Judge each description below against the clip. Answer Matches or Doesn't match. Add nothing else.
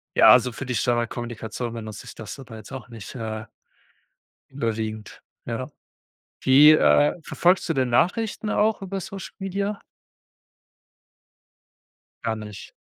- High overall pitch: Doesn't match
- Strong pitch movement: Matches